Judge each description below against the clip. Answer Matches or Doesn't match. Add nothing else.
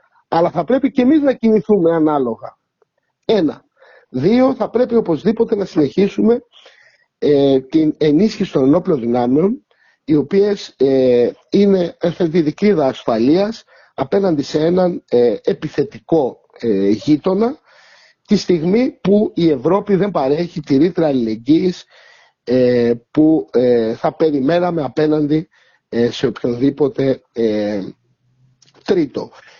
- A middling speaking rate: Doesn't match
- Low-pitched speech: Doesn't match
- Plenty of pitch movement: Matches